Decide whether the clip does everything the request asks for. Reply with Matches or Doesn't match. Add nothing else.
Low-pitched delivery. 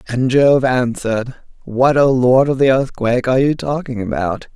Matches